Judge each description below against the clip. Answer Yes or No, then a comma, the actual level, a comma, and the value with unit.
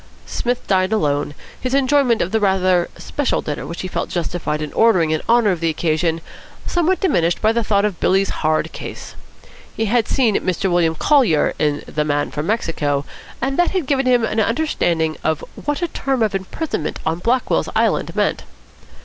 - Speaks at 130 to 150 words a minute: No, average, 185 wpm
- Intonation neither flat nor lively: No, wide, 7.3 semitones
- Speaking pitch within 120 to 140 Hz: No, high, 195 Hz